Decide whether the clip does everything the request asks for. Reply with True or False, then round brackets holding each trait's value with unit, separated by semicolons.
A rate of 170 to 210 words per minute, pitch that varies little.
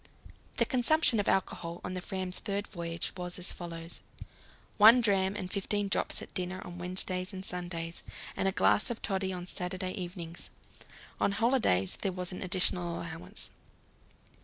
False (160 wpm; 2.1 semitones)